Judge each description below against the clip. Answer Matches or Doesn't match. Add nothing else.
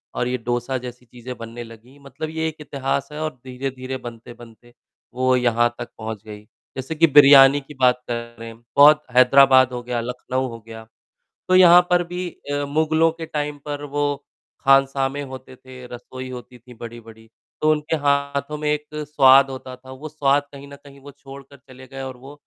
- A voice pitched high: Doesn't match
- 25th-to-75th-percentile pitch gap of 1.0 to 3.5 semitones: Matches